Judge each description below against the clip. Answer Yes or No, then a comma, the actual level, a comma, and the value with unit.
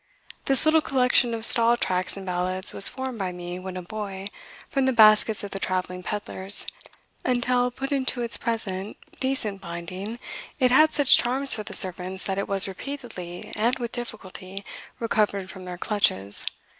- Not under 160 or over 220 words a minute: Yes, average, 170 wpm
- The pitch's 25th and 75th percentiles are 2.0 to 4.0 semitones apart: No, average, 4.8 semitones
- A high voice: Yes, high, 210 Hz